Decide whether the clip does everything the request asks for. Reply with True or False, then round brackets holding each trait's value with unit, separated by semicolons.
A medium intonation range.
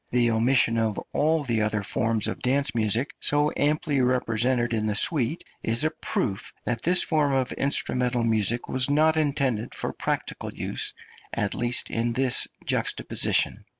True (3.8 semitones)